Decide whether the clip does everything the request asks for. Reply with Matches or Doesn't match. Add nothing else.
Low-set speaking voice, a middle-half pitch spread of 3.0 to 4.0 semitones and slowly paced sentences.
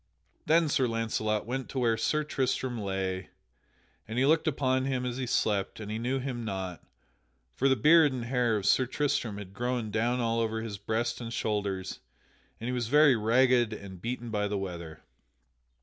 Doesn't match